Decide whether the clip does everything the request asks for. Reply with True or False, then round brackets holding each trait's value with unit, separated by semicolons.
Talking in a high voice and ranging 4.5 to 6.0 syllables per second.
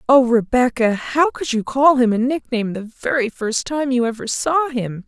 True (250 Hz; 4.7 syllables/s)